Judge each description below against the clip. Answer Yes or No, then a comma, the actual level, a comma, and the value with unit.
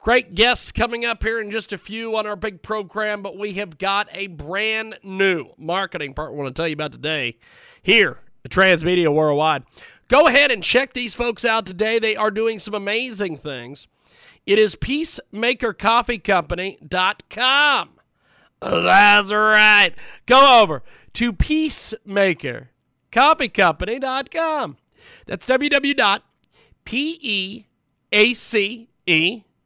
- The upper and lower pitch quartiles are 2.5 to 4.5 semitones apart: Yes, average, 4.1 semitones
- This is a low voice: No, high, 210 Hz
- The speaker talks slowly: Yes, slow, 125 wpm